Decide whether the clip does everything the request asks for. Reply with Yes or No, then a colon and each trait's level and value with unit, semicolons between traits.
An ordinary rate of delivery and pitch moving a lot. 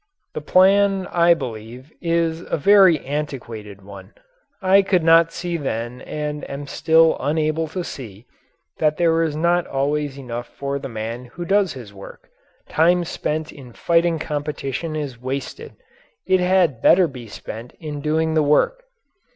No: average, 150 wpm; average, 4.5 semitones